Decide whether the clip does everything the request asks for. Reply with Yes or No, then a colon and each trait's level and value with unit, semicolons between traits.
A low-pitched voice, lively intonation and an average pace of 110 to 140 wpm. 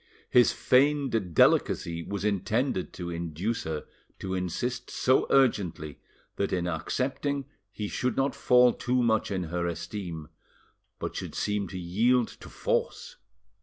Yes: low, 100 Hz; wide, 6.2 semitones; slow, 135 wpm